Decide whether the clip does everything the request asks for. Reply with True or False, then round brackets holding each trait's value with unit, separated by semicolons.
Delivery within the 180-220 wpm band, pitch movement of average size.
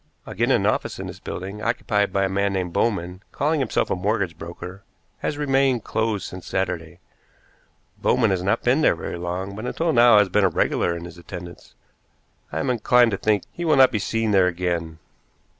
True (190 wpm; 4.5 semitones)